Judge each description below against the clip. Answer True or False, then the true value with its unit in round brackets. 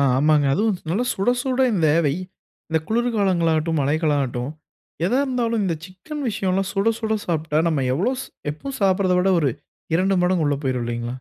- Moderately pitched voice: True (180 Hz)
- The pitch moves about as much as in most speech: False (5.9 semitones)